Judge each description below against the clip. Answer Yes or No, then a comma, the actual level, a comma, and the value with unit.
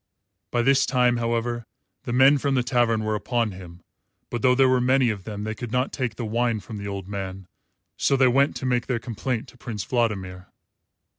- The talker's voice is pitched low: Yes, low, 120 Hz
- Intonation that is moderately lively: Yes, average, 3.0 semitones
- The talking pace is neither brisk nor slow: No, fast, 210 wpm